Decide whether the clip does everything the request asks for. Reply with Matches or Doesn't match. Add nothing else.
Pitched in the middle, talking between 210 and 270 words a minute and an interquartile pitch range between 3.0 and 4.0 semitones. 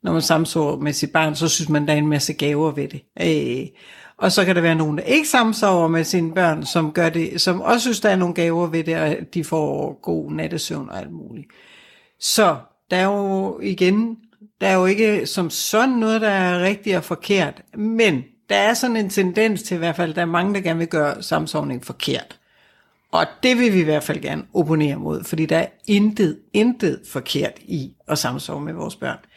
Doesn't match